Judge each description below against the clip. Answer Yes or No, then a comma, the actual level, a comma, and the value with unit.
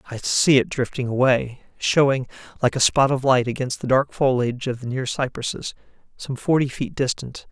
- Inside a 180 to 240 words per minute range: Yes, average, 185 wpm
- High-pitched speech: No, low, 130 Hz